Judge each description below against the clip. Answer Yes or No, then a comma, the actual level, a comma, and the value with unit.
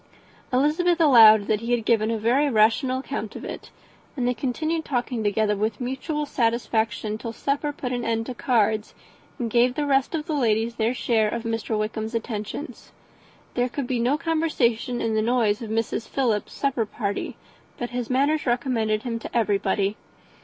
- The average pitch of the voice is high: Yes, high, 235 Hz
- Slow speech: No, average, 175 wpm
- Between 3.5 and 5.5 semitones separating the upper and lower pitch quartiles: No, average, 3.1 semitones